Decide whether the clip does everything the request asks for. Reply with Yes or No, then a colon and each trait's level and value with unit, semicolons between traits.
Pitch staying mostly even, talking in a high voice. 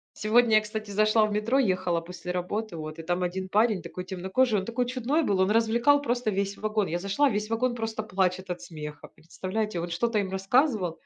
No: average, 3.8 semitones; high, 210 Hz